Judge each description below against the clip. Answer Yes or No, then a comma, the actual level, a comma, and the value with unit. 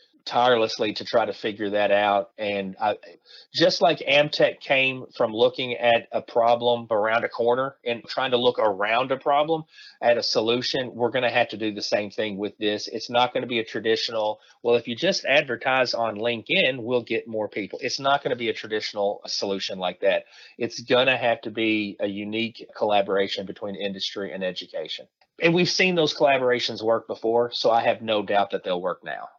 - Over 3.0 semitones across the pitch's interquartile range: No, average, 2.7 semitones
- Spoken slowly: No, average, 200 wpm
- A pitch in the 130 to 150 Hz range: No, low, 115 Hz